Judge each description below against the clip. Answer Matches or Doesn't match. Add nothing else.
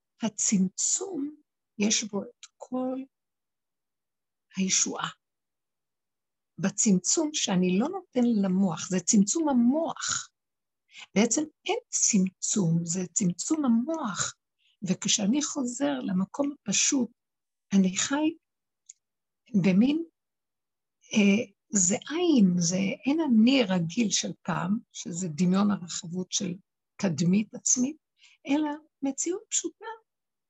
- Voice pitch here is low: Doesn't match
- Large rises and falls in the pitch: Matches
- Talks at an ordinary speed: Doesn't match